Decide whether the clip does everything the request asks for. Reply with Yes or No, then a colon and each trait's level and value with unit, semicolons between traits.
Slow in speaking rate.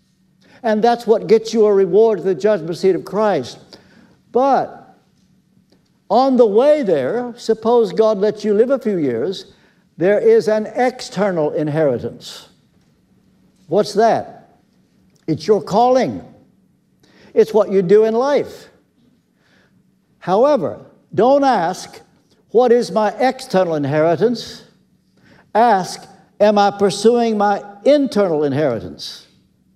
Yes: slow, 115 wpm